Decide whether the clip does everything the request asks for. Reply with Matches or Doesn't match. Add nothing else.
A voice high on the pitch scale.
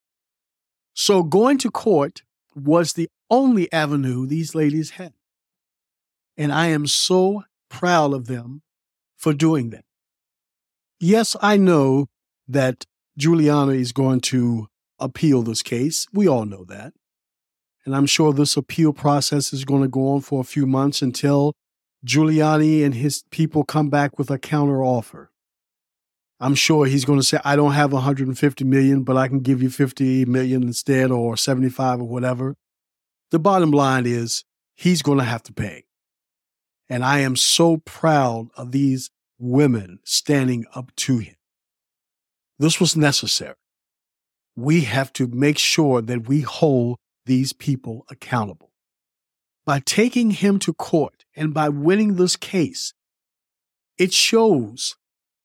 Doesn't match